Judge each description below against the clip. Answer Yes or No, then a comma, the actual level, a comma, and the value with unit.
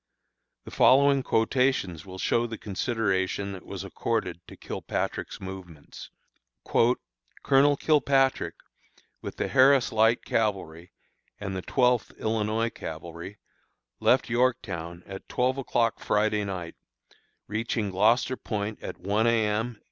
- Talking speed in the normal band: No, slow, 120 wpm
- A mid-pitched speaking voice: No, low, 110 Hz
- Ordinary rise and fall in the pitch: Yes, average, 4.5 semitones